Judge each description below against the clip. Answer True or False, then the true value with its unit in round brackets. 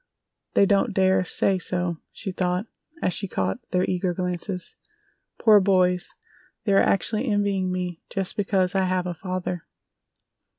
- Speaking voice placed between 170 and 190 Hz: True (185 Hz)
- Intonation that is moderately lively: False (1.6 semitones)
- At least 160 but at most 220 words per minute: False (145 wpm)